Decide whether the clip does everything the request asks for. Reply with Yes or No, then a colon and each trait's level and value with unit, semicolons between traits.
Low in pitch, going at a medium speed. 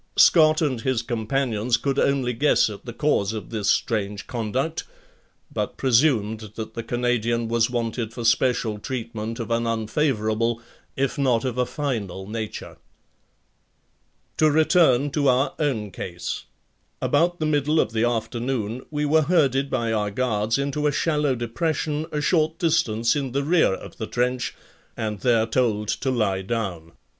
Yes: low, 120 Hz; average, 155 wpm